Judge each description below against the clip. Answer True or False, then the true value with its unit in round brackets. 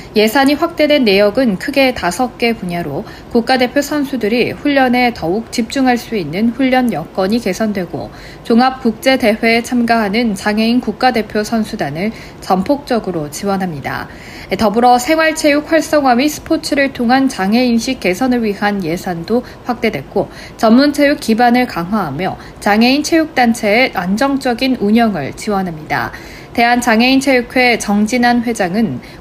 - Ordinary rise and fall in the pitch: True (4.4 semitones)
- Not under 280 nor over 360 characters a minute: True (320 characters per minute)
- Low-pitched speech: False (235 Hz)